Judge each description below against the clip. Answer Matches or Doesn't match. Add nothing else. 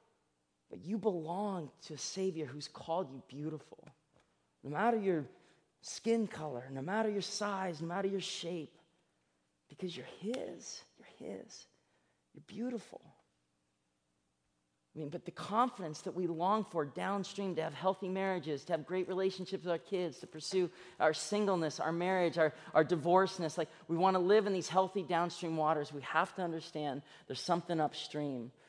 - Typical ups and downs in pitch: Matches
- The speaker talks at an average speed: Matches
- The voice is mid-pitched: Matches